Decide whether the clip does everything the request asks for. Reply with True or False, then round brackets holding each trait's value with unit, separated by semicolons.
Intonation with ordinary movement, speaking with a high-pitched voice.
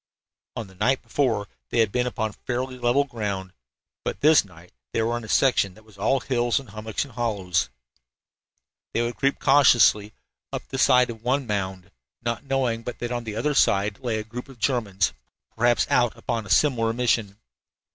False (3.0 semitones; 115 Hz)